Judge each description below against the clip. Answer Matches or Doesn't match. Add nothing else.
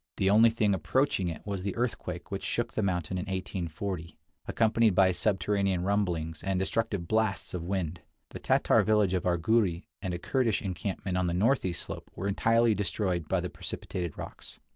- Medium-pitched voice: Doesn't match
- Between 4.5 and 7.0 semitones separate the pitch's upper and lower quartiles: Doesn't match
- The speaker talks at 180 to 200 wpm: Matches